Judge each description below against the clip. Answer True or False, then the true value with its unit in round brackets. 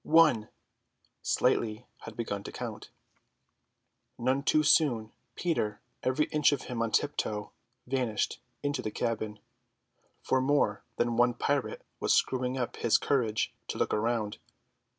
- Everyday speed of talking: False (130 wpm)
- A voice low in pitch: True (120 Hz)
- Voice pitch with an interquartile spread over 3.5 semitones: True (4.2 semitones)